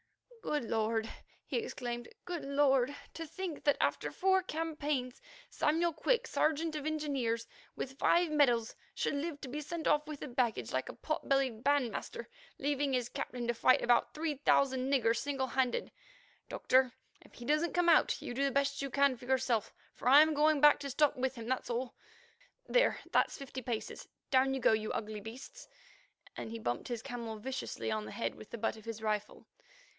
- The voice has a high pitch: Yes, very high, 265 Hz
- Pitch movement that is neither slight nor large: Yes, average, 4.0 semitones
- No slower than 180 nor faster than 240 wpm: Yes, average, 190 wpm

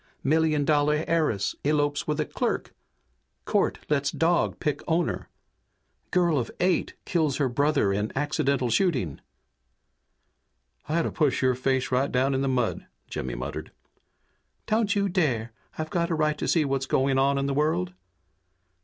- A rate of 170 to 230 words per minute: No, average, 155 wpm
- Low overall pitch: No, medium, 145 Hz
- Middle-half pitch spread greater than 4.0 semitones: No, average, 3.4 semitones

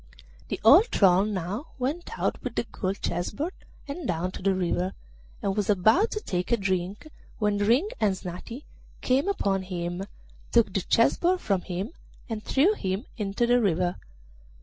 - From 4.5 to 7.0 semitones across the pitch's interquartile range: Yes, average, 5.3 semitones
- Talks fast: No, average, 170 wpm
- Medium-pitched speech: No, high, 205 Hz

